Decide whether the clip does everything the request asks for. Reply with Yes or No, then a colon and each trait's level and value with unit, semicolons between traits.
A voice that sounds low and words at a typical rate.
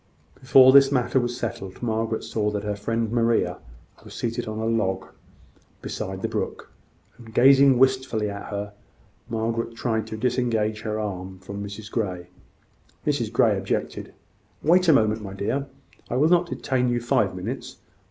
Yes: low, 115 Hz; average, 160 wpm